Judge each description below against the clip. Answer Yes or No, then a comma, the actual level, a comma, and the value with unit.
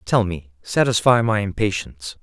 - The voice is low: Yes, low, 100 Hz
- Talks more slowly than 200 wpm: Yes, slow, 135 wpm